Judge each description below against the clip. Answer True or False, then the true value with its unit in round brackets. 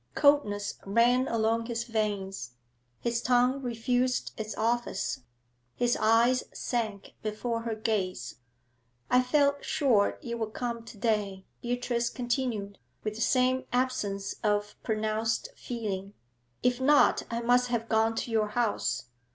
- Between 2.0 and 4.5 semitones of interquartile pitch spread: True (2.6 semitones)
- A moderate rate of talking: False (130 wpm)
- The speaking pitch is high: True (230 Hz)